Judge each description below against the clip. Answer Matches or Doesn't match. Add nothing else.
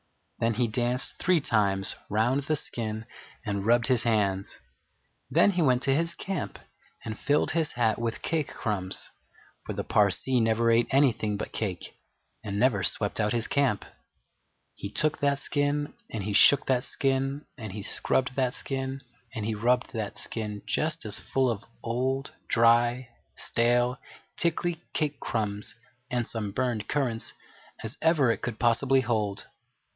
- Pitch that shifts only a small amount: Doesn't match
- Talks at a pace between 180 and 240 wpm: Doesn't match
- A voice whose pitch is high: Doesn't match